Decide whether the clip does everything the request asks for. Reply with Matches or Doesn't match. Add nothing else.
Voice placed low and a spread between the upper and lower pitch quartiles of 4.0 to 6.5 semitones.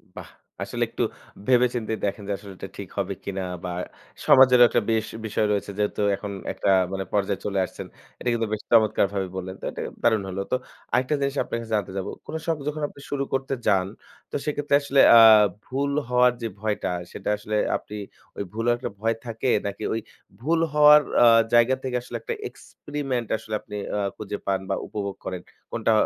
Matches